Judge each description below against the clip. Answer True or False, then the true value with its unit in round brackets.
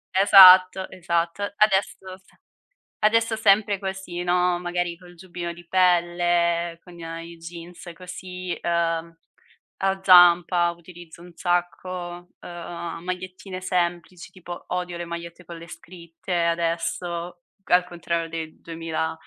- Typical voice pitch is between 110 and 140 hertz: False (175 Hz)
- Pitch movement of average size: False (1.3 semitones)